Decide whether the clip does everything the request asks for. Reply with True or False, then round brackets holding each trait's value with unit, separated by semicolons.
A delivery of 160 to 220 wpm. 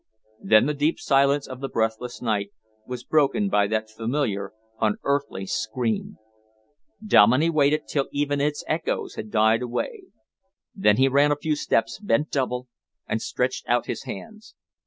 False (150 wpm)